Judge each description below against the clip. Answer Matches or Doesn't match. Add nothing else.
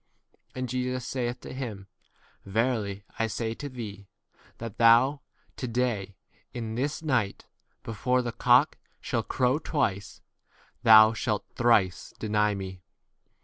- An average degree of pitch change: Matches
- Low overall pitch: Matches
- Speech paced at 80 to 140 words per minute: Matches